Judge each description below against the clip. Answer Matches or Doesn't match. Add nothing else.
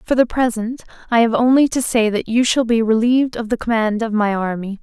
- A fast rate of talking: Matches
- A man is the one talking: Doesn't match